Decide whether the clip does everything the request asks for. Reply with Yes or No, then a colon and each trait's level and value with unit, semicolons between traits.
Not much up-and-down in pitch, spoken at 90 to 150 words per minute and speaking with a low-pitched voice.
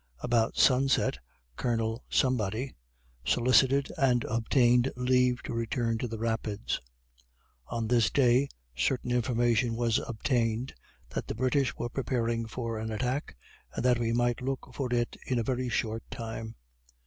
Yes: narrow, 1.9 semitones; slow, 135 wpm; low, 120 Hz